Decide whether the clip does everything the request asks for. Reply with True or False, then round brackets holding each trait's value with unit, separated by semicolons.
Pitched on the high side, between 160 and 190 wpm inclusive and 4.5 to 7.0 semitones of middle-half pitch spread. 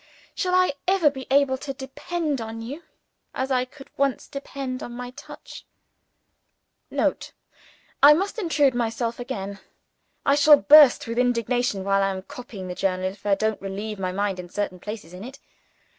True (245 Hz; 170 wpm; 5.6 semitones)